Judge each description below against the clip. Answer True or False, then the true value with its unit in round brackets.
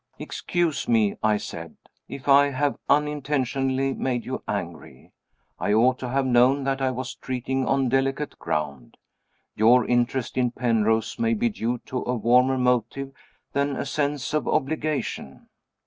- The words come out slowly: False (145 wpm)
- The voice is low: True (130 Hz)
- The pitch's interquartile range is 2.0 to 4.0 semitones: True (2.5 semitones)